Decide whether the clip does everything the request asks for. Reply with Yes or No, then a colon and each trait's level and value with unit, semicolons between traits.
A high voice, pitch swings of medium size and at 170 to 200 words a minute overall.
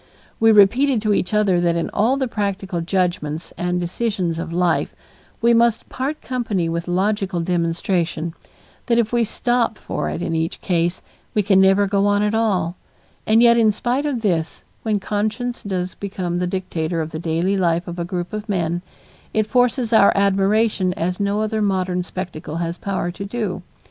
Yes: high, 195 Hz; average, 3.8 semitones; average, 180 wpm